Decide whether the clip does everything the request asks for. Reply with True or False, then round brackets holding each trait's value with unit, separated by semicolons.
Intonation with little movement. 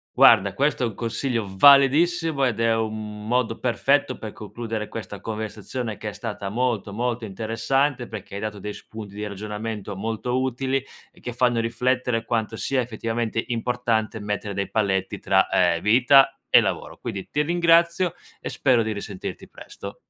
False (3.1 semitones)